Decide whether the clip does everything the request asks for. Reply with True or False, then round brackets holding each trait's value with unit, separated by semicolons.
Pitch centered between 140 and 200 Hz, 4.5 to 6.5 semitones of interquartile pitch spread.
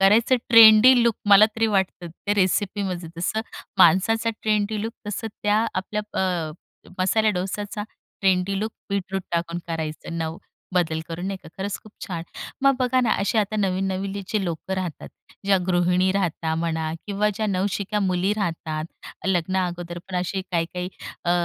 False (190 Hz; 3.1 semitones)